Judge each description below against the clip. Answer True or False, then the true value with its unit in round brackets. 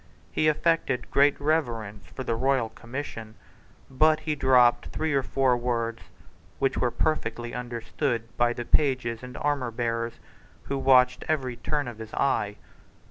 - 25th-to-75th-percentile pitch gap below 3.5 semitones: True (3.1 semitones)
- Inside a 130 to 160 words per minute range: True (140 wpm)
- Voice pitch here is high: False (125 Hz)